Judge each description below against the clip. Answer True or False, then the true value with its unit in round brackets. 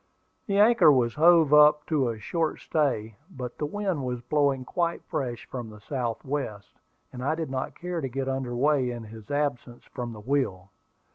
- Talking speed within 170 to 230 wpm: True (190 wpm)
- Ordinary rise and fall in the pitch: True (4.0 semitones)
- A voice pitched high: False (135 Hz)